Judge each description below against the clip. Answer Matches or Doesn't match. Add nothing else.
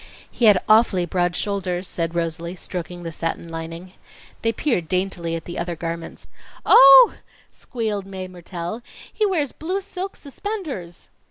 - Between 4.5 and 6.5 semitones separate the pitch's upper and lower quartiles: Matches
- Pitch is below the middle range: Doesn't match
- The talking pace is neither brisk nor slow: Matches